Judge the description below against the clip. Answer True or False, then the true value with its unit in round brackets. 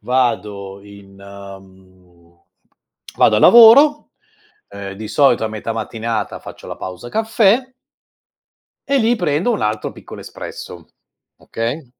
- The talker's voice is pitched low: True (110 Hz)